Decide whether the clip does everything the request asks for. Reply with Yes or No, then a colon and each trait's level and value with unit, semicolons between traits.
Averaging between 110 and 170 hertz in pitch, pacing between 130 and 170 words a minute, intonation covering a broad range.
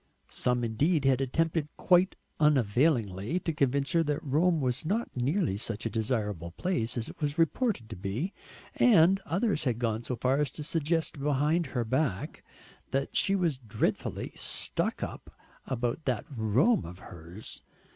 Yes: low, 135 Hz; average, 155 wpm; wide, 6.1 semitones